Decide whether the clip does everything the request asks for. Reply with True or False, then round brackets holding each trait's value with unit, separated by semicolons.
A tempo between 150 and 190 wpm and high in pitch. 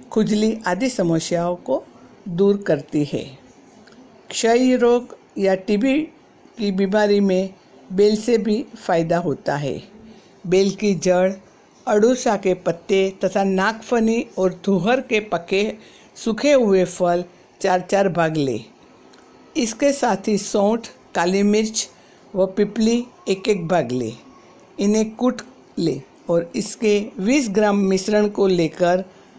False (125 wpm; 200 Hz)